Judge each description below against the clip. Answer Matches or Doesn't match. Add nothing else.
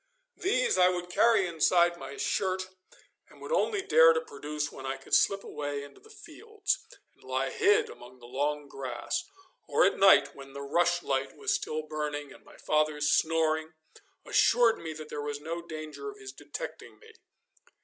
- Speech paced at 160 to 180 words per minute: Matches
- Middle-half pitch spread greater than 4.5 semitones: Matches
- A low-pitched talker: Doesn't match